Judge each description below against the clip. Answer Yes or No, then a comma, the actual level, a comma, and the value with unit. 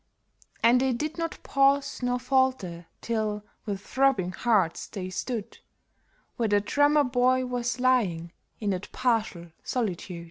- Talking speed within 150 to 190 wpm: No, slow, 135 wpm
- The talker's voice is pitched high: Yes, high, 235 Hz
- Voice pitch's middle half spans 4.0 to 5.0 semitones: Yes, average, 4.5 semitones